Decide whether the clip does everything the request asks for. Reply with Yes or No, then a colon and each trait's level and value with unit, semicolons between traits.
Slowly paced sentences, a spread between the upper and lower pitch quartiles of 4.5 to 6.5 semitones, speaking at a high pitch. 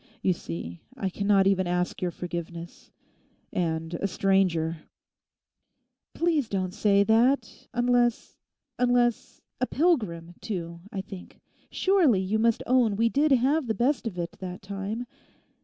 Yes: slow, 120 wpm; wide, 5.4 semitones; high, 200 Hz